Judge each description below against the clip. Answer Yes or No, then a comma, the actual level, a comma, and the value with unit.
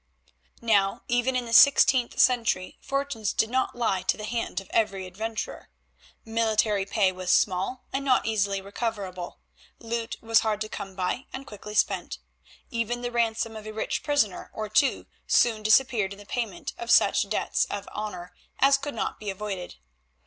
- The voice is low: No, high, 220 Hz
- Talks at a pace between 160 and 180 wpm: Yes, average, 170 wpm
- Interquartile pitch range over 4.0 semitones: No, average, 3.3 semitones